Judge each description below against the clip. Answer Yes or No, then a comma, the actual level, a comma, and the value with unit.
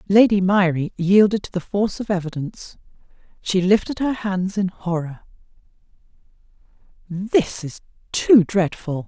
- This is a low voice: No, high, 190 Hz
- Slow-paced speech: Yes, slow, 120 wpm